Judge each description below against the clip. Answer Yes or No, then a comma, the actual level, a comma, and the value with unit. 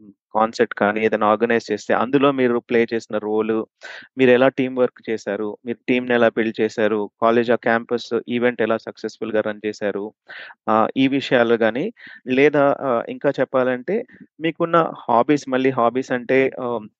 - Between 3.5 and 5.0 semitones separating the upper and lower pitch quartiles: No, average, 2.9 semitones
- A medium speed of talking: No, fast, 140 wpm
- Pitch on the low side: Yes, low, 115 Hz